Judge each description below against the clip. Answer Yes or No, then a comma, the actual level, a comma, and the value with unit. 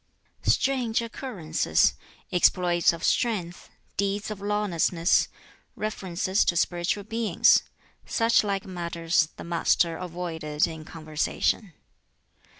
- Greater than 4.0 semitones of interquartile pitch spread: No, average, 3.7 semitones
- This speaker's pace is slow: Yes, slow, 95 wpm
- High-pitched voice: No, medium, 180 Hz